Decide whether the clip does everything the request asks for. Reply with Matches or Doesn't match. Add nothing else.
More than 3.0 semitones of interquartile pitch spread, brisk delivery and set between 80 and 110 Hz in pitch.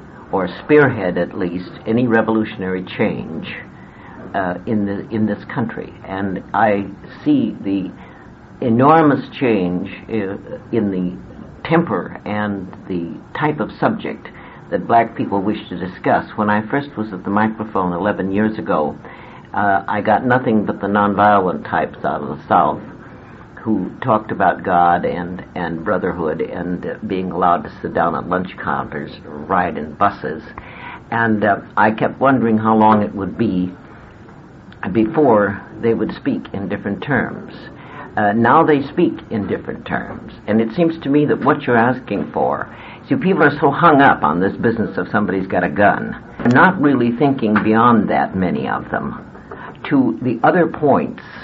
Doesn't match